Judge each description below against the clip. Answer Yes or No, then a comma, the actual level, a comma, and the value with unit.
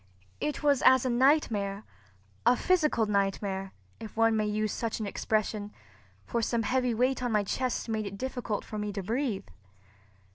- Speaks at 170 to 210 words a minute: No, average, 160 wpm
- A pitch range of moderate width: Yes, average, 3.7 semitones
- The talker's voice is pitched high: Yes, high, 220 Hz